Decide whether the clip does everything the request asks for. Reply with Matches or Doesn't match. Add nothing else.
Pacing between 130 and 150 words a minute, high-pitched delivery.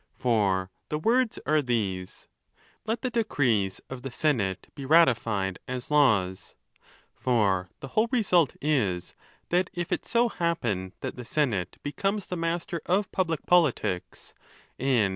Doesn't match